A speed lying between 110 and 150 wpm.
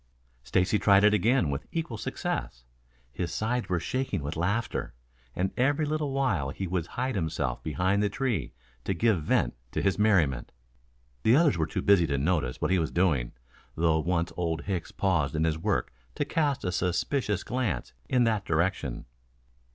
No: average, 175 wpm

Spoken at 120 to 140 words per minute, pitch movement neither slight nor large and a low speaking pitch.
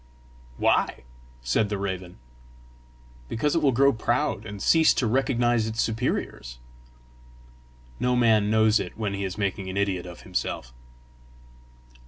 Yes: slow, 135 wpm; average, 3.7 semitones; low, 110 Hz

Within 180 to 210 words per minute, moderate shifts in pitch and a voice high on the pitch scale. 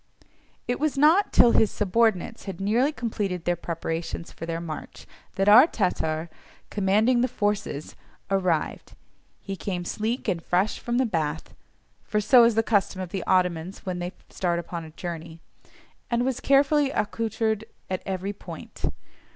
No: average, 155 wpm; average, 4.9 semitones; high, 195 Hz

